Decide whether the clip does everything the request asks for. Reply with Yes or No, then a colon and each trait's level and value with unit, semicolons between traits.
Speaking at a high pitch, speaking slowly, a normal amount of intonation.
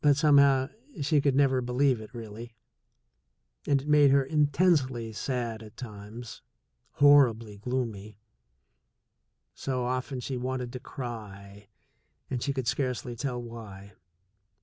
No: low, 125 Hz; slow, 125 wpm; average, 3.4 semitones